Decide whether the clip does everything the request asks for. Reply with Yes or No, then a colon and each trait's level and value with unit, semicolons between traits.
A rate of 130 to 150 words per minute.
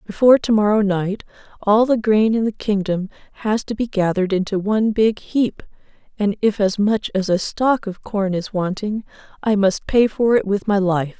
No: average, 200 wpm